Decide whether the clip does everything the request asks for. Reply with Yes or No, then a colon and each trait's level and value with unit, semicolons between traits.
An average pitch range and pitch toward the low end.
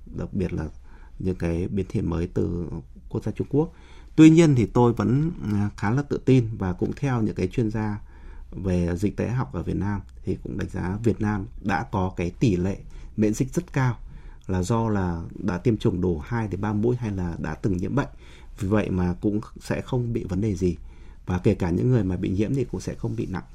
Yes: average, 4.4 semitones; low, 100 Hz